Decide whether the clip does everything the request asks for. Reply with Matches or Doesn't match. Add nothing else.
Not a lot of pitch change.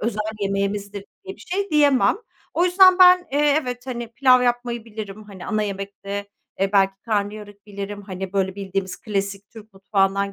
Doesn't match